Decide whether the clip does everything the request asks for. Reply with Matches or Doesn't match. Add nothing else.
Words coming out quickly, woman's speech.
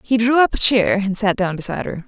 Matches